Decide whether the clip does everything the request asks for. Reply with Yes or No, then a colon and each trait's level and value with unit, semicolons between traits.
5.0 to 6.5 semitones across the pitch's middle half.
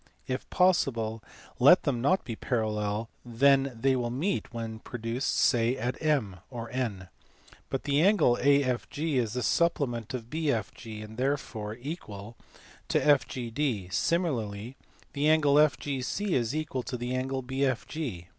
No: average, 3.8 semitones